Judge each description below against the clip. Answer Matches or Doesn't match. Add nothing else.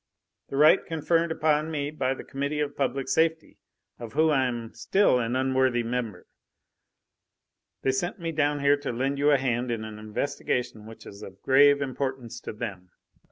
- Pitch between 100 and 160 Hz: Matches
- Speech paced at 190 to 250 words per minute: Doesn't match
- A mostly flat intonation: Doesn't match